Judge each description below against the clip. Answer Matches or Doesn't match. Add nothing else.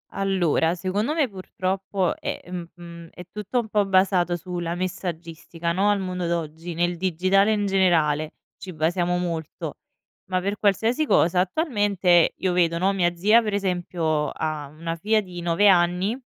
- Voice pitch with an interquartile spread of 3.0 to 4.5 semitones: Doesn't match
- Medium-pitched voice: Matches